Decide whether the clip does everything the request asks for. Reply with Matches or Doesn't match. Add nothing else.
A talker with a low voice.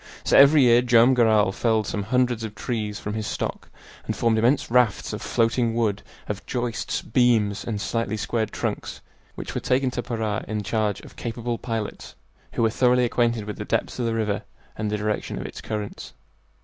Matches